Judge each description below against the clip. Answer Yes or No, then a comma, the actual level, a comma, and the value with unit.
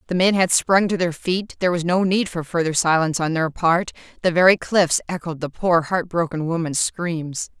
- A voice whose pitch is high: No, medium, 170 Hz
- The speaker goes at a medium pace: No, fast, 215 wpm